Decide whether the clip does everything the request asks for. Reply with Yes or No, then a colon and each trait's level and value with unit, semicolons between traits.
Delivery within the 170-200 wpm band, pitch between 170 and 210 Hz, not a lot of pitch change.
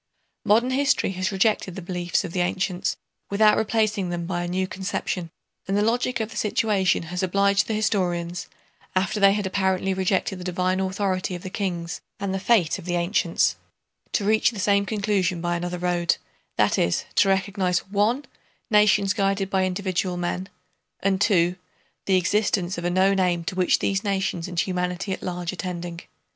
Yes: average, 180 wpm; high, 190 Hz; narrow, 2.1 semitones